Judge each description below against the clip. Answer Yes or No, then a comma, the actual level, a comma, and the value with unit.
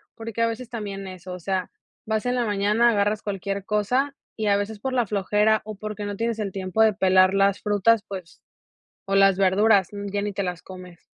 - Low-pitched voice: No, high, 205 Hz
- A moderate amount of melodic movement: No, narrow, 2.1 semitones